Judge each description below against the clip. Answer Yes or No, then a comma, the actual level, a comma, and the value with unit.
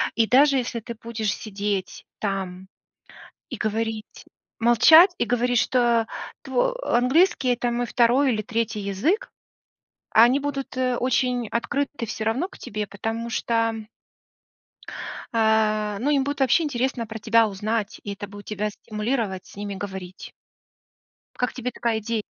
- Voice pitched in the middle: No, high, 230 Hz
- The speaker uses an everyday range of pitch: Yes, average, 3.1 semitones